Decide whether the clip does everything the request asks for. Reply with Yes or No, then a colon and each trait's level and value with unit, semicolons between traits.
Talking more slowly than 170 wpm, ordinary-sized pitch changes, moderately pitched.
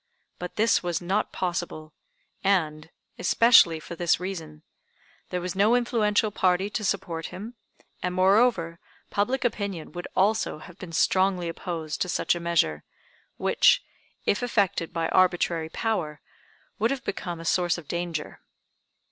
Yes: average, 140 wpm; average, 3.4 semitones; medium, 180 Hz